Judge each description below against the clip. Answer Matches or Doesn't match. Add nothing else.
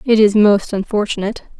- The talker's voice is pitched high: Matches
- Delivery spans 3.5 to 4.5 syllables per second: Doesn't match